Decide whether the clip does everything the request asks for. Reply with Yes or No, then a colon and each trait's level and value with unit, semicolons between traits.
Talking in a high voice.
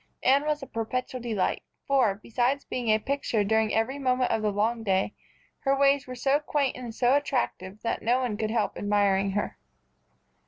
Yes: high, 240 Hz